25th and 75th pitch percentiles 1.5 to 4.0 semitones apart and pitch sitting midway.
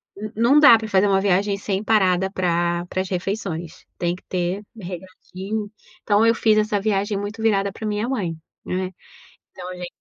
No: average, 2.8 semitones; high, 195 Hz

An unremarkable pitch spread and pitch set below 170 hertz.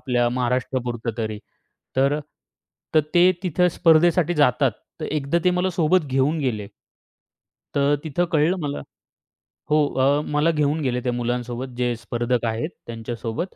Yes: average, 4.5 semitones; low, 135 Hz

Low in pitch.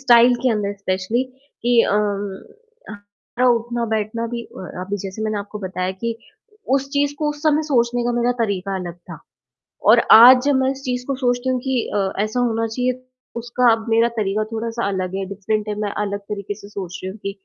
No: high, 225 Hz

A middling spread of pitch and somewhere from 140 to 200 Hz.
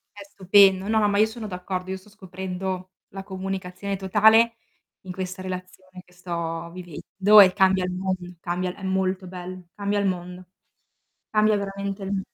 No: narrow, 1.6 semitones; high, 190 Hz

